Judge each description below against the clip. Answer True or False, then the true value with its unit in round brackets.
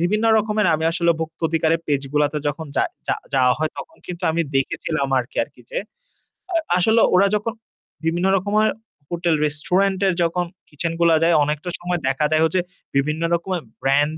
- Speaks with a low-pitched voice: False (165 Hz)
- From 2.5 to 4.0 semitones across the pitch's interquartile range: True (3.4 semitones)